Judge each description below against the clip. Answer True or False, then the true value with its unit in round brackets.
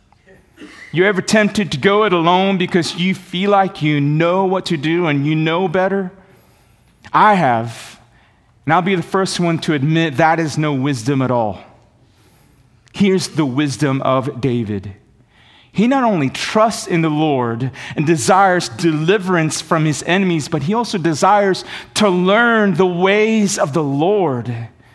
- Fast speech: False (155 wpm)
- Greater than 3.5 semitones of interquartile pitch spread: True (5.1 semitones)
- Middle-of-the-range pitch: True (165 Hz)